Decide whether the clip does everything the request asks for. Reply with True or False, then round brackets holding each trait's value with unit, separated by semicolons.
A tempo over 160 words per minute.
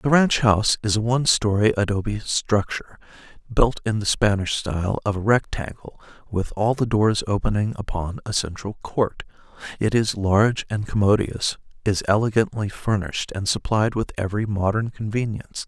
False (155 wpm)